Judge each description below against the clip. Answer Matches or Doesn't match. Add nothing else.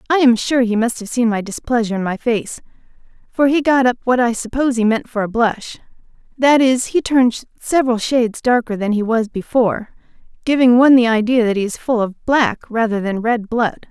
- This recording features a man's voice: Doesn't match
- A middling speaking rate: Doesn't match